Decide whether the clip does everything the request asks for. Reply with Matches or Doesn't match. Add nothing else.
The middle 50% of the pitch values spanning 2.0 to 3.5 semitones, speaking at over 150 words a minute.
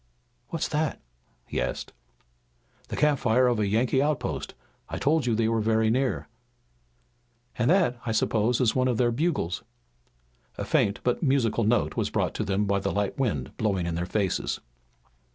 Doesn't match